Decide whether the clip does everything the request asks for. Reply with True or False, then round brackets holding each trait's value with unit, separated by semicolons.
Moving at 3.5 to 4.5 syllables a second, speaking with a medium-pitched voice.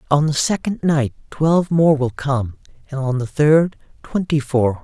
True (4.4 syllables/s; 145 Hz)